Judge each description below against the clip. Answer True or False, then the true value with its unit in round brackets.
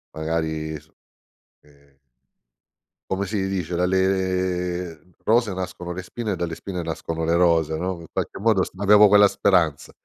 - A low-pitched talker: True (90 Hz)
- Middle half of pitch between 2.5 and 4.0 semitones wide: True (2.8 semitones)